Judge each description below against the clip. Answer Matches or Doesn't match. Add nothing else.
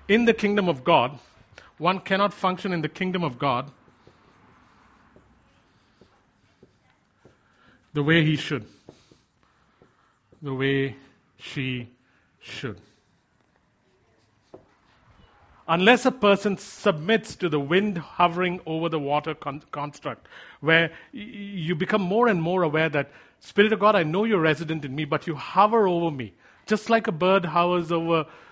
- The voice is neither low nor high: Matches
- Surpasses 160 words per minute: Doesn't match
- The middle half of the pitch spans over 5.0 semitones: Matches